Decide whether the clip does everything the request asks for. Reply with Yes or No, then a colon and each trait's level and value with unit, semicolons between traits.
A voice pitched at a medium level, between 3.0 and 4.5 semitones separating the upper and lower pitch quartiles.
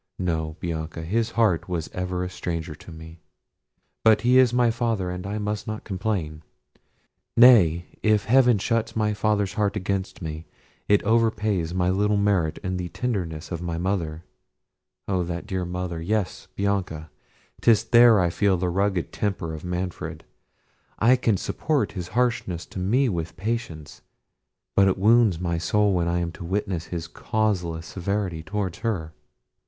No: very low, 95 Hz; average, 4.0 semitones